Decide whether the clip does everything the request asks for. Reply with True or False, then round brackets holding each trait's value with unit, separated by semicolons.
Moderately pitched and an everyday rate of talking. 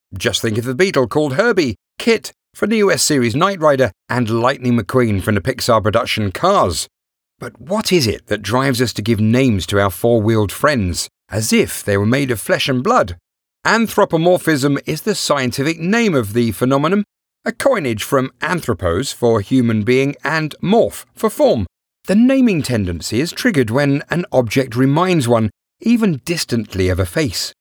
False (130 Hz; 170 wpm)